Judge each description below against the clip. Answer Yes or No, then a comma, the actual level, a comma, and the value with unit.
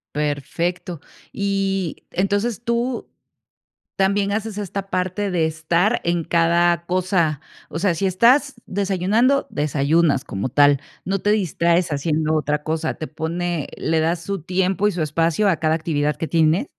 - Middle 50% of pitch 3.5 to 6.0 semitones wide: Yes, average, 3.8 semitones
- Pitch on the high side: No, medium, 175 Hz